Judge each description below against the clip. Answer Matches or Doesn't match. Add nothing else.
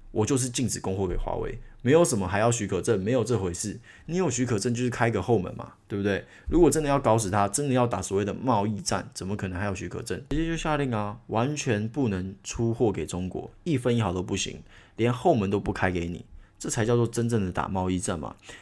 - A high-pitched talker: Doesn't match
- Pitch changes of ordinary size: Matches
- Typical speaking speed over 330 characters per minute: Matches